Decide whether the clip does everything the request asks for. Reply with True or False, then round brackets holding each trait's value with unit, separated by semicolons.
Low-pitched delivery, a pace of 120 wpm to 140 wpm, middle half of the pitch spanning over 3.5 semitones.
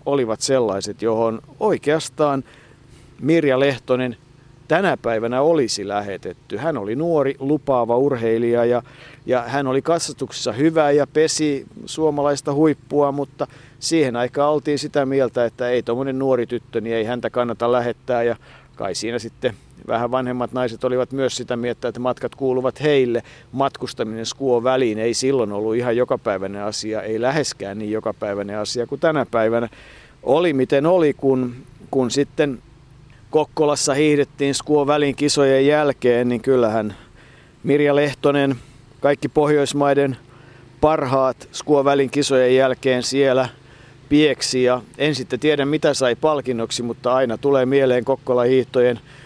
False (130 Hz; 130 wpm; 3.0 semitones)